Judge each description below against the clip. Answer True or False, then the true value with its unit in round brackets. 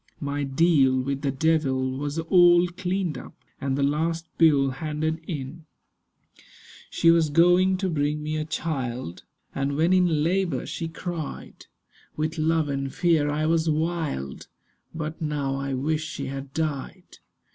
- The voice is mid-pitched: True (155 Hz)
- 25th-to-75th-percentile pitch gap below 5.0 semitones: True (3.1 semitones)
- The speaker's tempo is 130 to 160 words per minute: True (145 wpm)